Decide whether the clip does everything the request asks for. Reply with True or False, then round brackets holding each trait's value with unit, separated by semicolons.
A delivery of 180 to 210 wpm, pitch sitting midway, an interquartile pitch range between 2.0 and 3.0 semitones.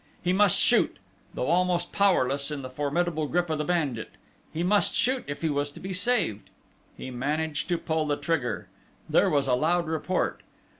False (185 wpm; 160 Hz; 3.7 semitones)